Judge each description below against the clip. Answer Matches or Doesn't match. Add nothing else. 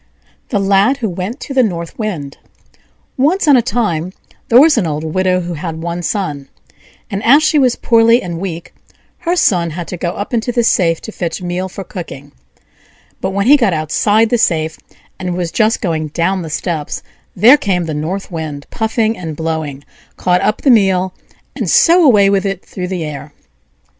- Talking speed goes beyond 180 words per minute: Matches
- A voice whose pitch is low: Doesn't match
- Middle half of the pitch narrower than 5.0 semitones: Doesn't match